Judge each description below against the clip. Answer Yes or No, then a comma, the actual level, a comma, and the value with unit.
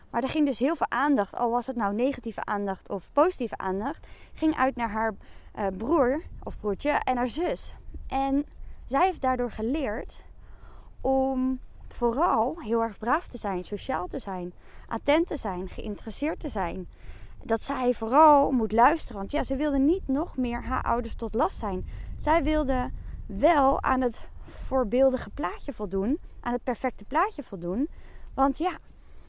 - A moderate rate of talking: Yes, average, 160 wpm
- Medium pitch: No, very high, 255 Hz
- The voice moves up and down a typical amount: Yes, average, 4.1 semitones